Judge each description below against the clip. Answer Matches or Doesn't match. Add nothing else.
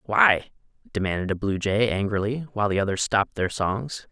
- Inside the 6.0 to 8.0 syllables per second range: Doesn't match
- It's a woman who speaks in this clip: Doesn't match